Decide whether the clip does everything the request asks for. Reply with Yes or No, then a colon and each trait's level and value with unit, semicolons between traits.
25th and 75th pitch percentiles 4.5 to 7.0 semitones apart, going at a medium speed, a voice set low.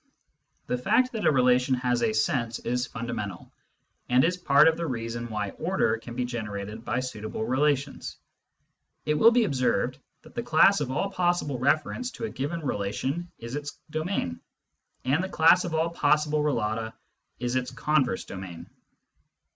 Yes: average, 5.2 semitones; average, 170 wpm; low, 130 Hz